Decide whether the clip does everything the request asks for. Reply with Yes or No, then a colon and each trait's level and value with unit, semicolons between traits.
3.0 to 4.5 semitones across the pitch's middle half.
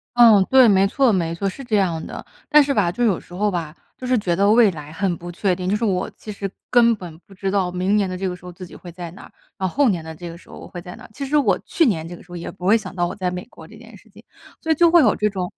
Yes: average, 3.8 semitones